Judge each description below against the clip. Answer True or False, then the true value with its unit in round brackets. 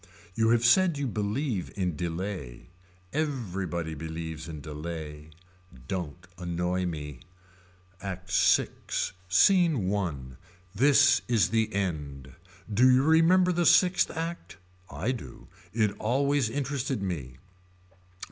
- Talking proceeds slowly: True (110 wpm)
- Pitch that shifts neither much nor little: False (8.5 semitones)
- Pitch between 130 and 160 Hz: False (95 Hz)